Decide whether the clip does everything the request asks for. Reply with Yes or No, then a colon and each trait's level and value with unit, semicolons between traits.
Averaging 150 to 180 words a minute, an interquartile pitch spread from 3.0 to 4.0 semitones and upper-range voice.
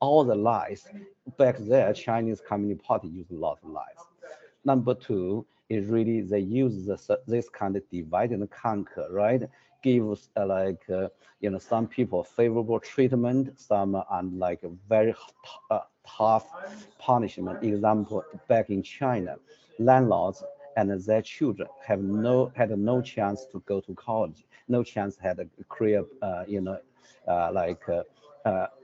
No: average, 155 wpm; average, 3.5 semitones; low, 110 Hz